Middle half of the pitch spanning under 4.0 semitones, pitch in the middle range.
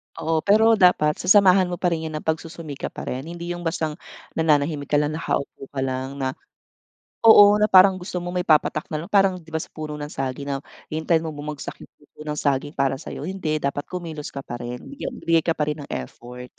Yes: average, 3.5 semitones; medium, 155 Hz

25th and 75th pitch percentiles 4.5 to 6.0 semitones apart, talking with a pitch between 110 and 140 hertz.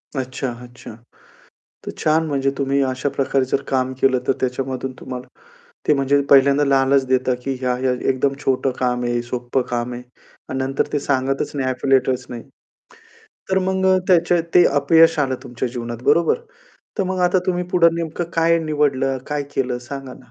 No: narrow, 2.5 semitones; low, 135 Hz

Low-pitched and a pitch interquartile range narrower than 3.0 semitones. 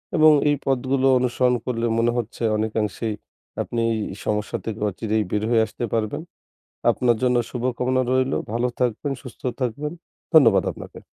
Yes: low, 120 Hz; narrow, 2.6 semitones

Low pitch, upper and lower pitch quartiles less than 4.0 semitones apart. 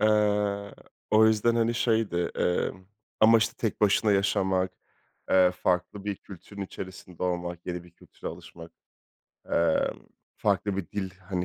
Yes: very low, 95 Hz; average, 2.8 semitones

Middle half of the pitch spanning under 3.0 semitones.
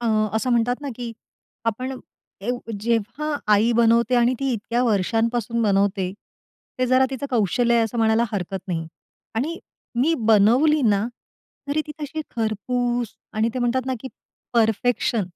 Yes: narrow, 2.6 semitones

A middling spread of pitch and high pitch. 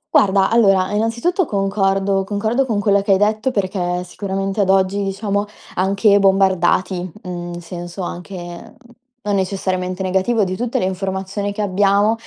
No: narrow, 1.7 semitones; high, 195 Hz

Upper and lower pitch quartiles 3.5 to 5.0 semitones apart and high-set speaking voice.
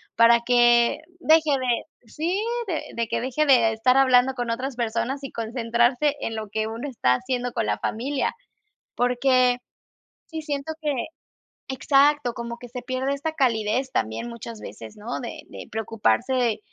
No: average, 2.8 semitones; high, 245 Hz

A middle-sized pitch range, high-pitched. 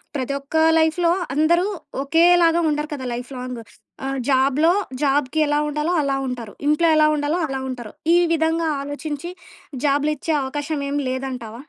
Yes: average, 3.3 semitones; very high, 290 Hz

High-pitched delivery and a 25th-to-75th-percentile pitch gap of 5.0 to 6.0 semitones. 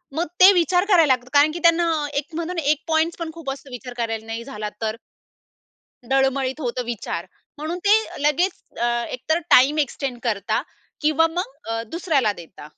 Yes: very high, 280 Hz; wide, 5.5 semitones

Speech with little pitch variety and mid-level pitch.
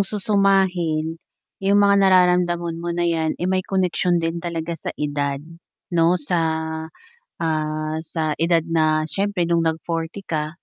Yes: narrow, 2.3 semitones; medium, 170 Hz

